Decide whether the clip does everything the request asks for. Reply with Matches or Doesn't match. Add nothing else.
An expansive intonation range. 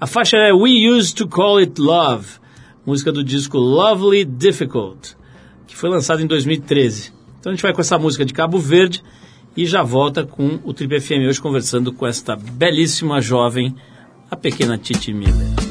Matches